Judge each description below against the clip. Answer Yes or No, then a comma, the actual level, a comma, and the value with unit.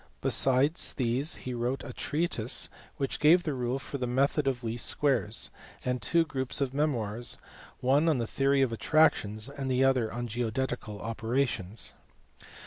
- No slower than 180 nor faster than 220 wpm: No, average, 155 wpm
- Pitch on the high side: No, low, 130 Hz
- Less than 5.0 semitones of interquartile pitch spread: Yes, average, 2.9 semitones